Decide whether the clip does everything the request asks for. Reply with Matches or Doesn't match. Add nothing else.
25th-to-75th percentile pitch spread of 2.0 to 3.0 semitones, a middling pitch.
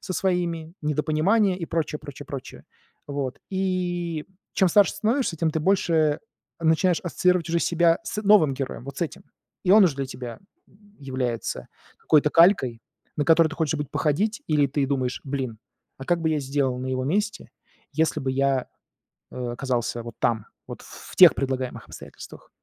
Doesn't match